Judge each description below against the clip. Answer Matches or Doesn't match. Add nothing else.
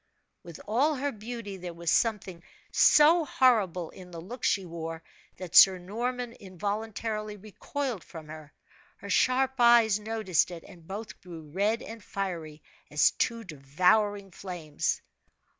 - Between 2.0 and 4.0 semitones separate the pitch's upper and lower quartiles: Doesn't match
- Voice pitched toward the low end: Doesn't match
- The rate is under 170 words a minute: Matches